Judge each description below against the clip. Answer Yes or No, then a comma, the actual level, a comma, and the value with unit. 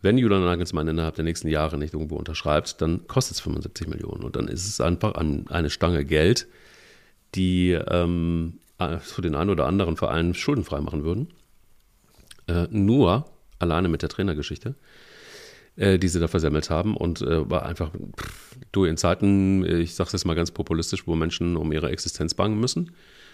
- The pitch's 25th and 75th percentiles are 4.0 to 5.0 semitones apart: No, average, 3.4 semitones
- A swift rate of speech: No, average, 170 wpm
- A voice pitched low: Yes, very low, 85 Hz